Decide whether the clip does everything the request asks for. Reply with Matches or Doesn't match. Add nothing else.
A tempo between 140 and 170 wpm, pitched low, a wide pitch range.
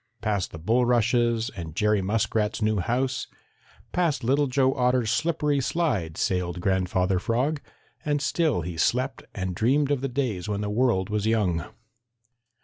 Matches